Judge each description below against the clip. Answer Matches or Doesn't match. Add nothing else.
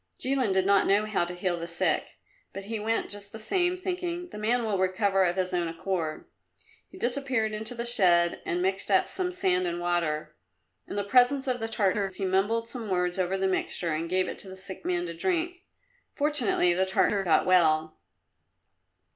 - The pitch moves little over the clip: Doesn't match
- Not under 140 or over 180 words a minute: Doesn't match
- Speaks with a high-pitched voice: Matches